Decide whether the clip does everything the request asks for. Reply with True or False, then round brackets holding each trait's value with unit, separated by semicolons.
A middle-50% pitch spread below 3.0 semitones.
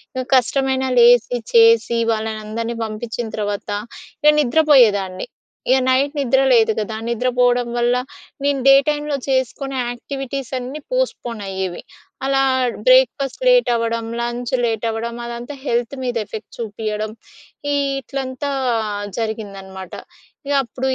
False (3.3 semitones)